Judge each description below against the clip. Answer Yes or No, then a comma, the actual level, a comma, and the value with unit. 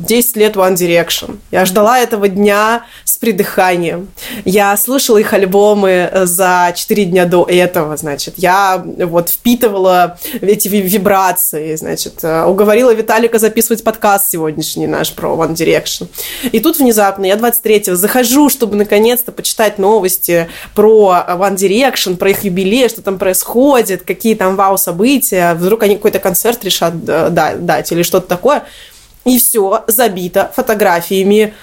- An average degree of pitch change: Yes, average, 3.5 semitones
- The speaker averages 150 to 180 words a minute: No, average, 135 wpm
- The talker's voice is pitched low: No, high, 200 Hz